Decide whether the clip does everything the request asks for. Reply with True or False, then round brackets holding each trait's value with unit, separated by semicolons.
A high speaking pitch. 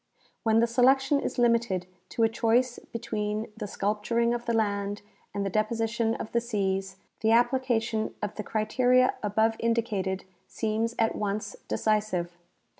True (225 Hz)